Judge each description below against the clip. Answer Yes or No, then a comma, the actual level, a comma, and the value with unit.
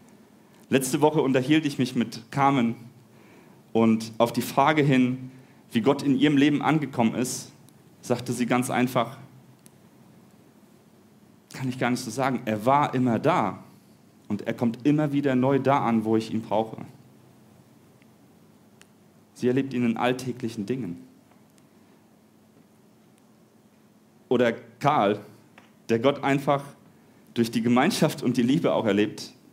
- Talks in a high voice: No, low, 125 Hz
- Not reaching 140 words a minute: Yes, average, 130 wpm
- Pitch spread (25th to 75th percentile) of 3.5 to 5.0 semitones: No, average, 2.9 semitones